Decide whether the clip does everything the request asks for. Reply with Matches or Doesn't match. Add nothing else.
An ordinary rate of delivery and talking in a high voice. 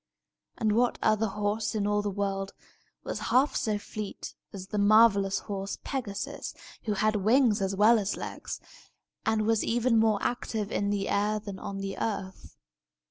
Matches